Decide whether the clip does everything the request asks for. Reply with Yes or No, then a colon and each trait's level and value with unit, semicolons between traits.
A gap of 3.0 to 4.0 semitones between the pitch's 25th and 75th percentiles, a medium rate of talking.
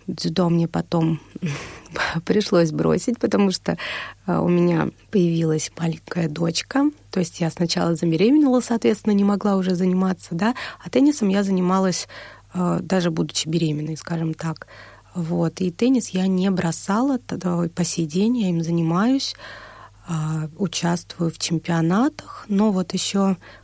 Yes: average, 3.3 semitones; average, 130 wpm